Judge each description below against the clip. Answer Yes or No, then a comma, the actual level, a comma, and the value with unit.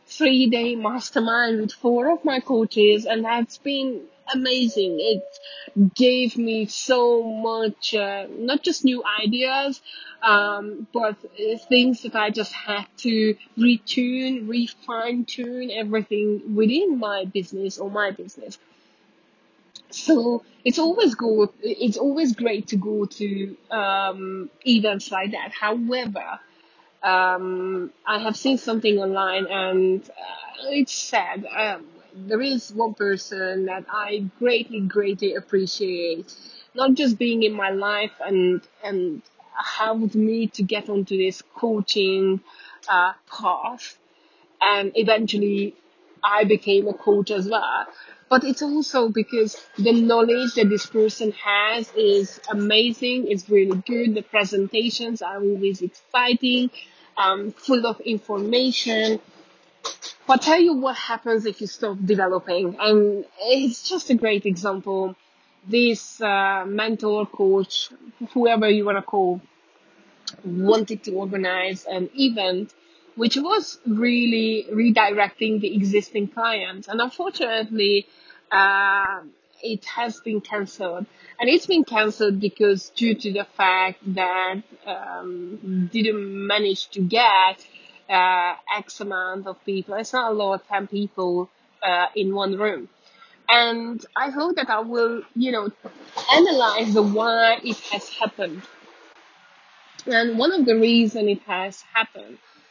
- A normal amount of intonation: Yes, average, 3.2 semitones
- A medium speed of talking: No, slow, 130 wpm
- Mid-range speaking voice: No, high, 215 Hz